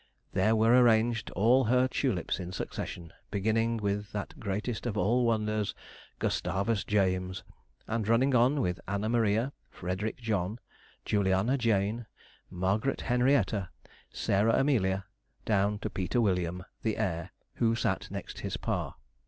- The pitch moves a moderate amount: Yes, average, 3.3 semitones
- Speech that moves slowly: Yes, slow, 130 wpm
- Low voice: Yes, low, 105 Hz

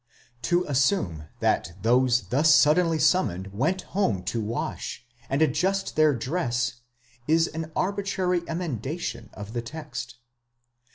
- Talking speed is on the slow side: Yes, slow, 120 wpm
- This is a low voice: No, medium, 145 Hz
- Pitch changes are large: Yes, wide, 6.5 semitones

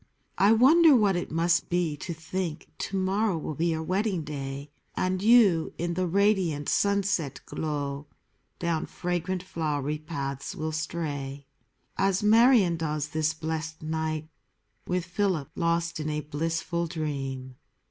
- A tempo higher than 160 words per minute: No, slow, 135 wpm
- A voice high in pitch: No, medium, 165 Hz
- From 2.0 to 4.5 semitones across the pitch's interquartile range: Yes, average, 3.6 semitones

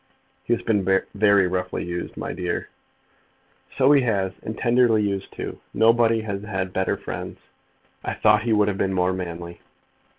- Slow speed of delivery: No, average, 165 wpm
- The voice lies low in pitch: Yes, low, 100 Hz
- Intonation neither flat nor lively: Yes, average, 3.2 semitones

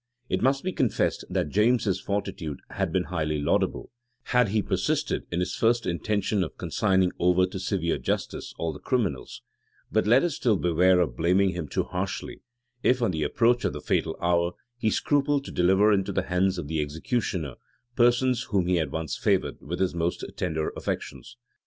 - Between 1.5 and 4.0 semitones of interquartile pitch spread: No, average, 4.6 semitones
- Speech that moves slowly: No, average, 185 wpm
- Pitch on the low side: Yes, very low, 95 Hz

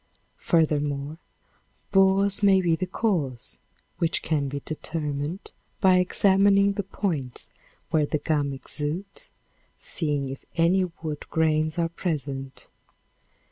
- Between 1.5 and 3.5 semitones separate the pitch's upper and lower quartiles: No, average, 4.5 semitones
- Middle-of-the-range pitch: Yes, medium, 160 Hz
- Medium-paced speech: No, slow, 110 wpm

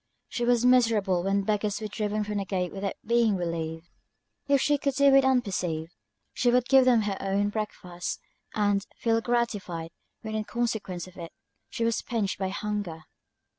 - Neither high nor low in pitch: No, high, 210 Hz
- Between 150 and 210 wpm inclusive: Yes, average, 170 wpm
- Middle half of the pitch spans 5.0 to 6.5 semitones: No, average, 4.0 semitones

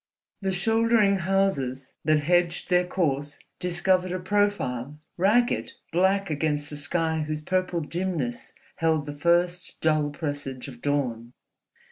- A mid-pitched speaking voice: Yes, medium, 165 Hz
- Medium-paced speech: No, slow, 125 wpm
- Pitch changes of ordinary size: Yes, average, 4.2 semitones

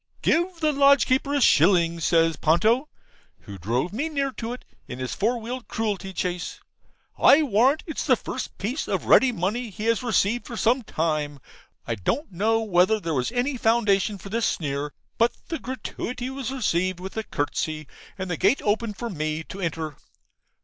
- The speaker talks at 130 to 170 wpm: No, average, 180 wpm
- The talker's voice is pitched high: Yes, high, 215 Hz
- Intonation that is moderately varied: No, wide, 6.9 semitones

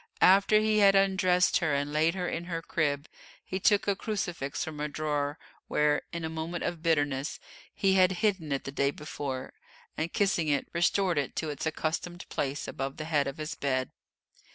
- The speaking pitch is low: No, medium, 160 Hz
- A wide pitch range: No, average, 3.9 semitones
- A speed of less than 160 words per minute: No, average, 190 wpm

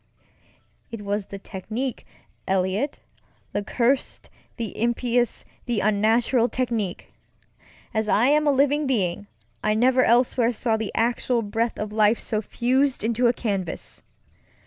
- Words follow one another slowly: Yes, slow, 125 wpm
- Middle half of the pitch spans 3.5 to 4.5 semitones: No, average, 2.9 semitones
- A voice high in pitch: Yes, high, 230 Hz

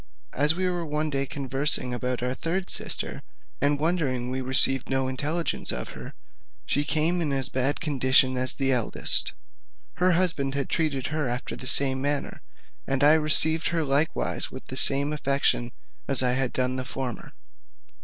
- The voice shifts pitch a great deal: No, average, 2.8 semitones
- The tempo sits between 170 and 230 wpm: Yes, average, 175 wpm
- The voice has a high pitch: No, medium, 140 Hz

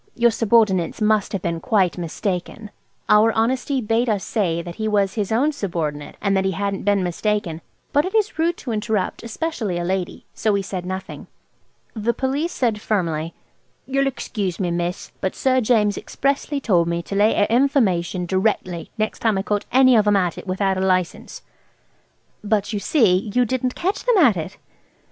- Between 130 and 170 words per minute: No, average, 185 wpm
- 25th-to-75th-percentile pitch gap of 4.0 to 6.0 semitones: Yes, average, 4.4 semitones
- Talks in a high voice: Yes, high, 210 Hz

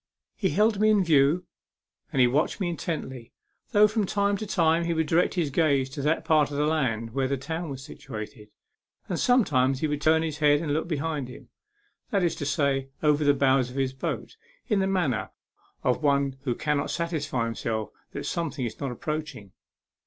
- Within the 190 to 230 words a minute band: Yes, average, 195 wpm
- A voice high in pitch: No, medium, 150 Hz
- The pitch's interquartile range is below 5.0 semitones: Yes, average, 3.9 semitones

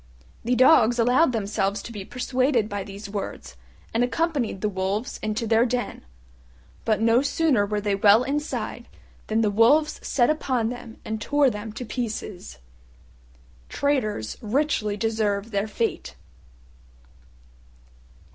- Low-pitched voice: No, high, 225 Hz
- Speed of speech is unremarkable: No, slow, 130 wpm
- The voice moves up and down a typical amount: Yes, average, 3.3 semitones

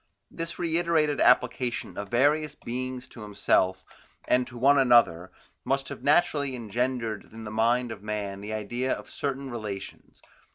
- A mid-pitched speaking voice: No, low, 125 Hz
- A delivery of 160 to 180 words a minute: No, average, 150 wpm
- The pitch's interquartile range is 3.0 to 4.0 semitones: No, average, 4.5 semitones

